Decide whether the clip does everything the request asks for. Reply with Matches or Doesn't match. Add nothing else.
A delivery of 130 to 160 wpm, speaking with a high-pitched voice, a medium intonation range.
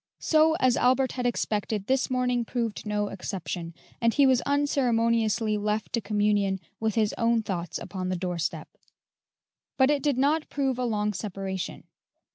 Matches